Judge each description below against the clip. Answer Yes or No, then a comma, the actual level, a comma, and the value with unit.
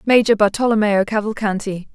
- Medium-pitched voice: No, high, 210 Hz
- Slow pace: Yes, slow, 90 wpm